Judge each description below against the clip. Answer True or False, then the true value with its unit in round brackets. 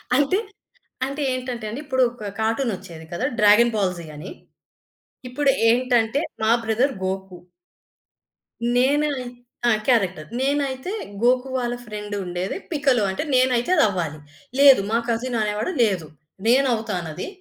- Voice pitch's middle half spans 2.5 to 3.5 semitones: False (4.4 semitones)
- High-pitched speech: True (235 Hz)